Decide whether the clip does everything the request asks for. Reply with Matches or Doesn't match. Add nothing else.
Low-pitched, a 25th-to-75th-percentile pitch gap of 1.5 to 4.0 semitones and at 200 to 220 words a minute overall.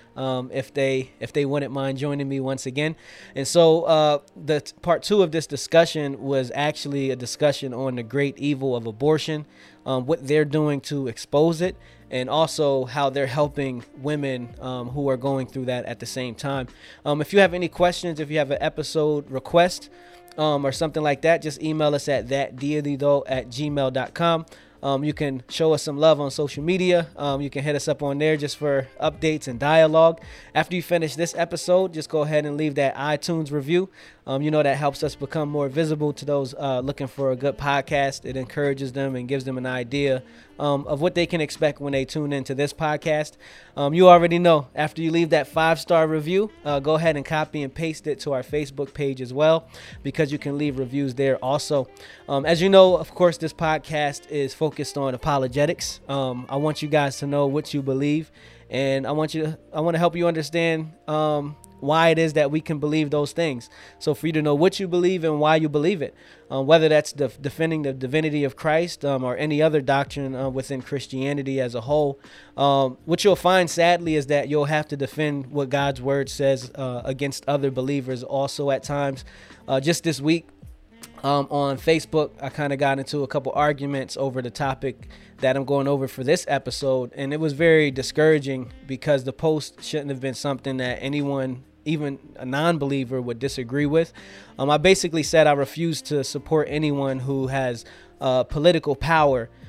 Doesn't match